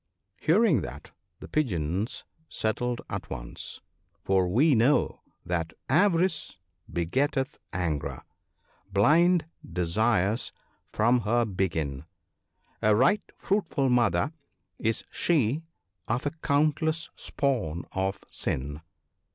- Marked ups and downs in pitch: Yes, wide, 8.7 semitones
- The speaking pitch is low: Yes, low, 115 Hz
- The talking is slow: Yes, slow, 100 wpm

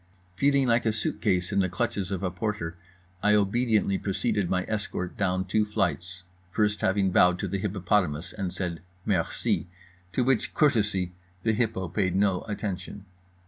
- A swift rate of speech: No, average, 155 wpm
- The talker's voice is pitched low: Yes, very low, 95 Hz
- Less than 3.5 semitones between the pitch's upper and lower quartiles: Yes, average, 2.8 semitones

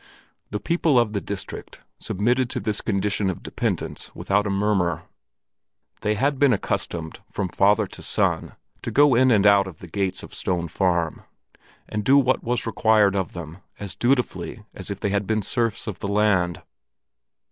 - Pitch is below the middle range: Yes, low, 105 Hz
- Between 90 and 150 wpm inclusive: No, average, 175 wpm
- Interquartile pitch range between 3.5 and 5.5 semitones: No, average, 3.1 semitones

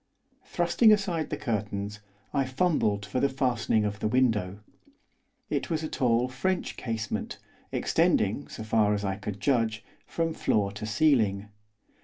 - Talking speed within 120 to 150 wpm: Yes, average, 145 wpm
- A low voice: Yes, low, 115 Hz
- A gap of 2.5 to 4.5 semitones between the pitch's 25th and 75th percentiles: No, average, 5.2 semitones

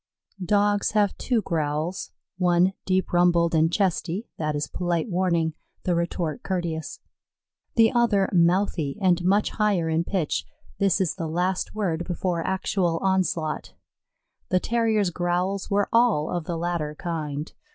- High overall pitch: No, medium, 175 Hz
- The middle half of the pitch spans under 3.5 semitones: Yes, average, 2.9 semitones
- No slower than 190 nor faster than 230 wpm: No, average, 140 wpm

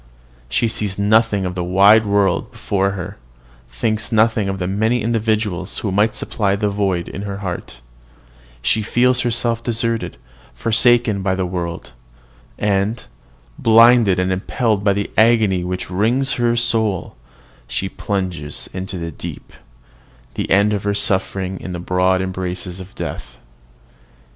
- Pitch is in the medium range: No, low, 100 Hz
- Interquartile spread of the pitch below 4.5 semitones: Yes, average, 3.2 semitones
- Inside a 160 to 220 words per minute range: No, average, 140 wpm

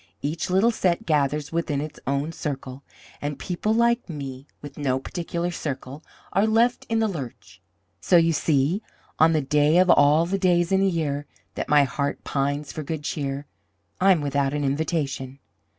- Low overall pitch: No, medium, 150 Hz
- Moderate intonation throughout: Yes, average, 3.7 semitones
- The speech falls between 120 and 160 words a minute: No, average, 170 wpm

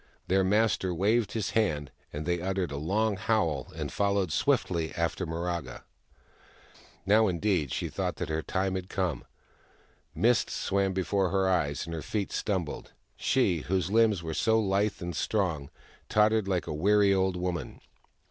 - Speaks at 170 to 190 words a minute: No, average, 155 wpm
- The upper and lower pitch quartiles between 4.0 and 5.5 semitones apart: No, average, 3.3 semitones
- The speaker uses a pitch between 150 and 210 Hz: No, very low, 95 Hz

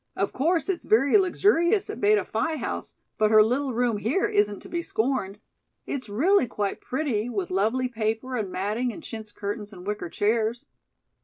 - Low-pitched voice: No, high, 235 Hz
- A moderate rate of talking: Yes, average, 175 wpm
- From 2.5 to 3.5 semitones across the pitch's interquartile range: No, wide, 5.4 semitones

